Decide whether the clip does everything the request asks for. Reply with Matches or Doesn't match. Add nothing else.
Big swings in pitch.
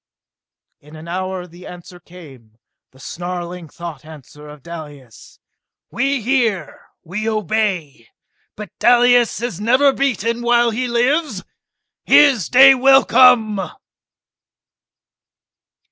Matches